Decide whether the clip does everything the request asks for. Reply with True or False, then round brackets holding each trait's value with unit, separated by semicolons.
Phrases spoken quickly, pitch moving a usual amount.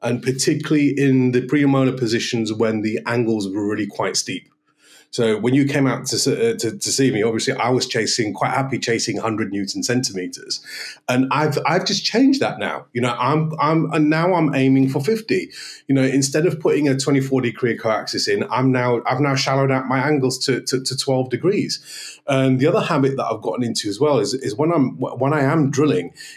True (210 wpm; 3.4 semitones)